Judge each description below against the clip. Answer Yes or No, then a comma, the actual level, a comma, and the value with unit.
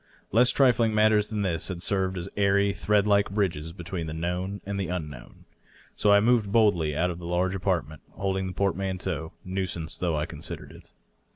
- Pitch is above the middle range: No, very low, 95 Hz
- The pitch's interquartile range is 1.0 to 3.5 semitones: Yes, average, 2.9 semitones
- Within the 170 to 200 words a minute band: Yes, average, 185 wpm